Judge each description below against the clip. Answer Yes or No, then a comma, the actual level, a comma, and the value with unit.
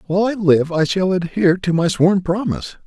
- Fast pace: Yes, fast, 210 wpm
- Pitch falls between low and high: Yes, medium, 180 Hz